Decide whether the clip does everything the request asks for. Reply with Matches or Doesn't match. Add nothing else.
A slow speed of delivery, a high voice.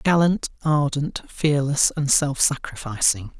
Doesn't match